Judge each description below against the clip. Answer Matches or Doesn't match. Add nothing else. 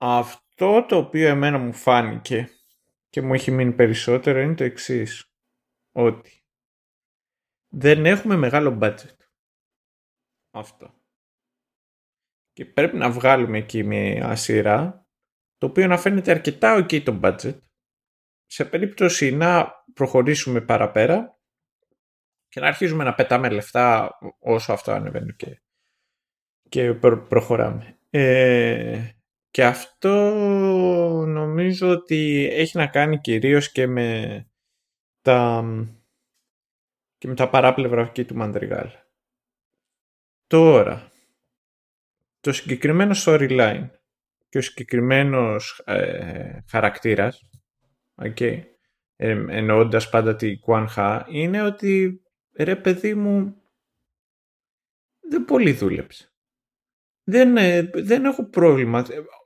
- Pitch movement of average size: Doesn't match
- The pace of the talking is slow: Matches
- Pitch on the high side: Doesn't match